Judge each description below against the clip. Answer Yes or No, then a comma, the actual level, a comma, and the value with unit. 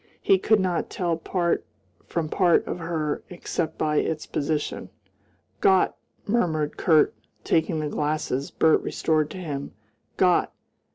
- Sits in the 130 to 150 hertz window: No, medium, 160 Hz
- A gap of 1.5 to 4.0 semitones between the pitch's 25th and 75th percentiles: Yes, average, 2.7 semitones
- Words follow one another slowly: Yes, slow, 130 wpm